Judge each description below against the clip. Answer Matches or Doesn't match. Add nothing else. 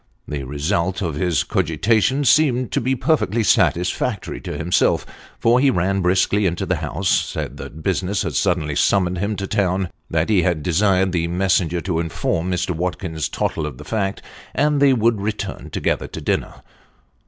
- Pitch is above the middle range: Doesn't match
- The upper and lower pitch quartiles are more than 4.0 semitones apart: Doesn't match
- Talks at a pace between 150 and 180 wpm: Matches